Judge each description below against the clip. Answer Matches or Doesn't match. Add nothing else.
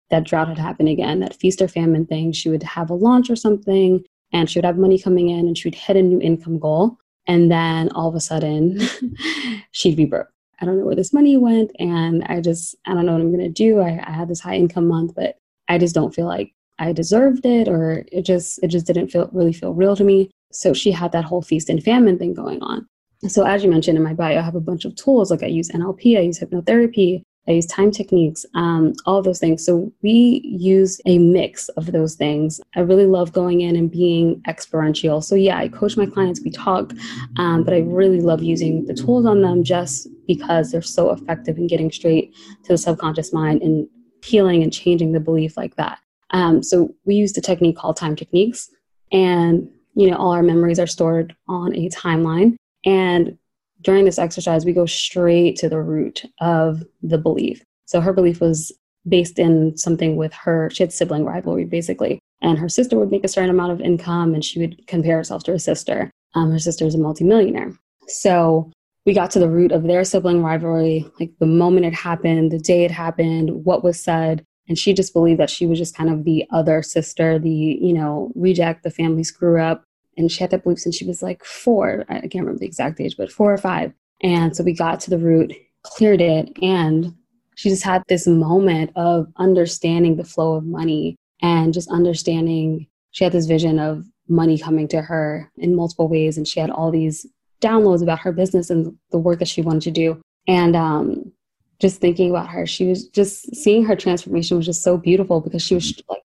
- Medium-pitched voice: Matches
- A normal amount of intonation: Doesn't match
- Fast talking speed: Matches